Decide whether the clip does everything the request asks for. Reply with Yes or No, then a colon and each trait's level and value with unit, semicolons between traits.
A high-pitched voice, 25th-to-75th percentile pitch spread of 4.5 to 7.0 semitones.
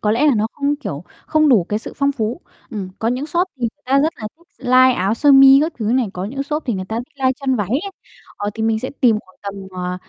Yes: high, 245 Hz; average, 4.8 semitones